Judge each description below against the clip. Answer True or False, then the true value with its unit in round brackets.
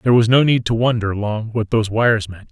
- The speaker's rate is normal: False (260 wpm)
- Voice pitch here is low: True (110 Hz)